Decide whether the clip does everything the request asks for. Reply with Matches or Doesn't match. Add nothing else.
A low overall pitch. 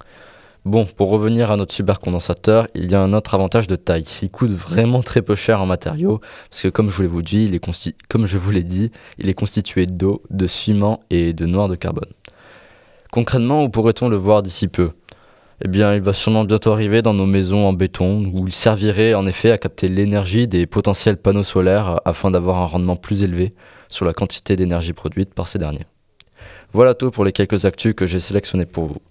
Matches